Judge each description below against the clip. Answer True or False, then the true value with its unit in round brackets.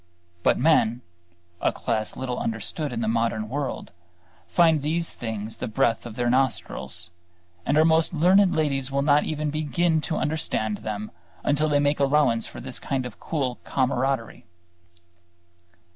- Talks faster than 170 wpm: False (150 wpm)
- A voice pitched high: False (135 Hz)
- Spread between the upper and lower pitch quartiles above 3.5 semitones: True (4.8 semitones)